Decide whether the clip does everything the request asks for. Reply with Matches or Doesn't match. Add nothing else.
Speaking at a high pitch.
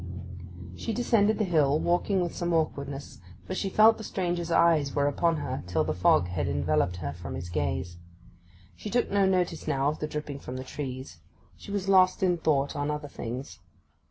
Doesn't match